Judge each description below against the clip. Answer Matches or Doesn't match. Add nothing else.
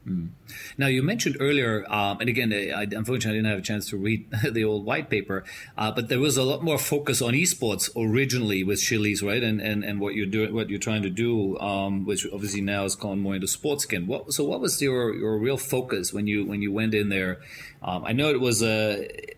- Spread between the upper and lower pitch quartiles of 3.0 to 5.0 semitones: Matches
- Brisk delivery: Matches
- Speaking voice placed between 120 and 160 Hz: Doesn't match